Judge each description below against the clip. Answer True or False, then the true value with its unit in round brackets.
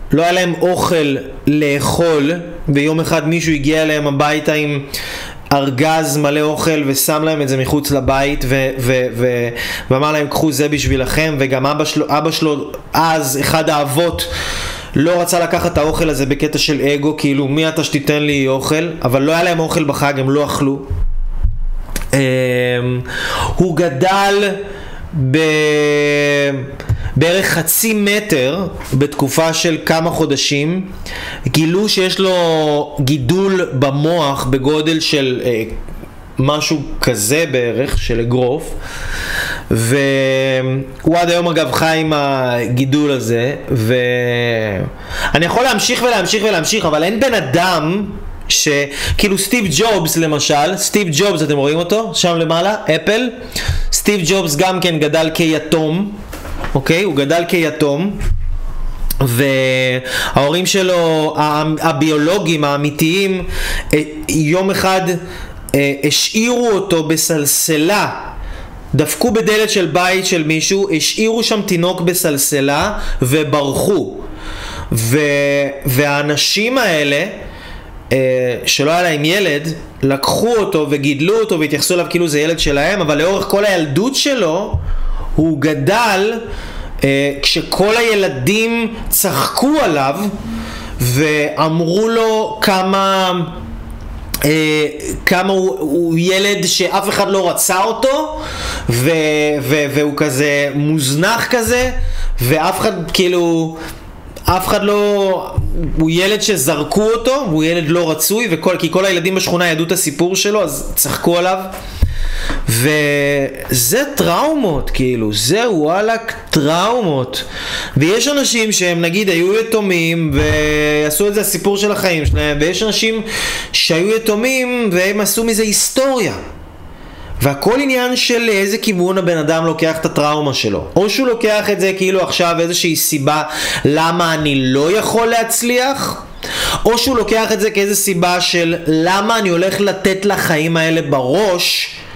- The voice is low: False (160 Hz)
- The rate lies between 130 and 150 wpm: False (120 wpm)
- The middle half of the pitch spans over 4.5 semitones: True (5.0 semitones)